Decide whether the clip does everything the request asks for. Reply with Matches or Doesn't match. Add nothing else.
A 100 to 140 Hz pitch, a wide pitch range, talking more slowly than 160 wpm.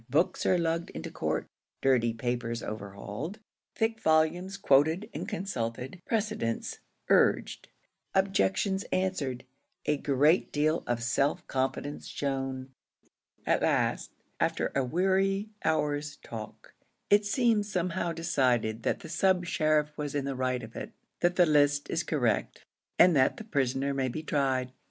Doesn't match